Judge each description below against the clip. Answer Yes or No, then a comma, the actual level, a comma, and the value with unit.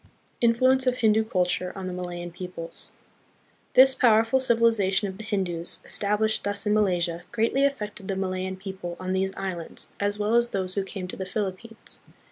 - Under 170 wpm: No, average, 175 wpm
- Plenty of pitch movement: No, average, 3.3 semitones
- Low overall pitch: No, high, 200 Hz